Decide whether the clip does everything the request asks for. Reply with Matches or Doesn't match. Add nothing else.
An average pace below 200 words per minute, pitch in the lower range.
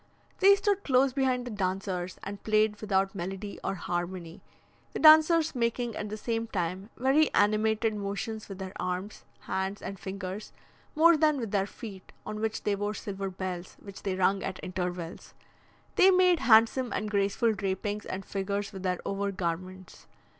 Doesn't match